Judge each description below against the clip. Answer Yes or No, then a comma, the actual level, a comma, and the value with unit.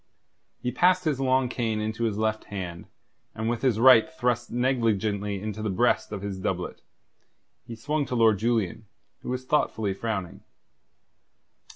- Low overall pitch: Yes, low, 115 Hz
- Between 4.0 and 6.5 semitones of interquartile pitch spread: No, average, 3.3 semitones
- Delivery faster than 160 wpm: No, average, 155 wpm